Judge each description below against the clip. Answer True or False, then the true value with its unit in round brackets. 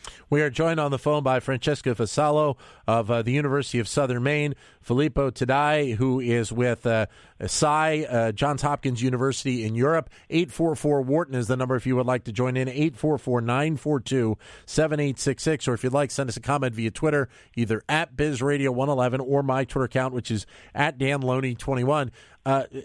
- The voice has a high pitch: False (135 Hz)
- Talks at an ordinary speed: True (165 wpm)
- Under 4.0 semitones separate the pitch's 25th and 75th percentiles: True (3.0 semitones)